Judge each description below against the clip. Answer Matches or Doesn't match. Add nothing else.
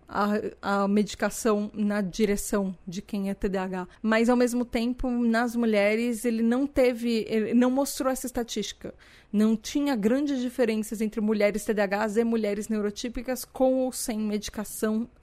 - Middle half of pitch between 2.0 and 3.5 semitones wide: Matches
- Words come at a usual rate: Matches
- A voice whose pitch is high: Matches